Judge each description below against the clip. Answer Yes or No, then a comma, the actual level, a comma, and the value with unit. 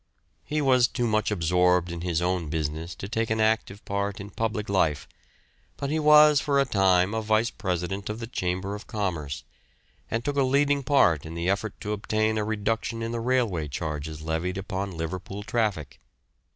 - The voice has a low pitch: Yes, low, 100 Hz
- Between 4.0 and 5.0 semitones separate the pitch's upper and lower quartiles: Yes, average, 4.3 semitones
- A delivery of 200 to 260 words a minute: No, average, 185 wpm